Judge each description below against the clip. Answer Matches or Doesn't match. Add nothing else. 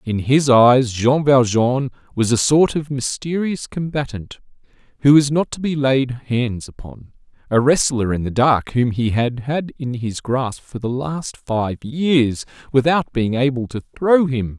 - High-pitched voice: Doesn't match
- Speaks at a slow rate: Doesn't match